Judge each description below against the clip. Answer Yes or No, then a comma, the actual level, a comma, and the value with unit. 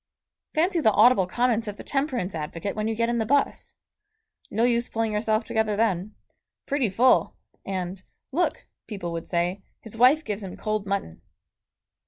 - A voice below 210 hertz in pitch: No, high, 215 Hz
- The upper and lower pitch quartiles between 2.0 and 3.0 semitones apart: No, average, 3.6 semitones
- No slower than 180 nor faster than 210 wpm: No, average, 165 wpm